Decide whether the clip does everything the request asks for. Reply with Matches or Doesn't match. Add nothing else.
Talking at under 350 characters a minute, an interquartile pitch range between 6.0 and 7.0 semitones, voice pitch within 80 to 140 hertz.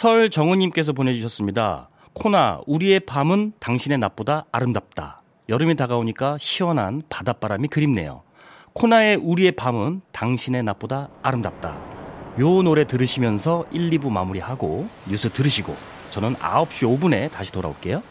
Matches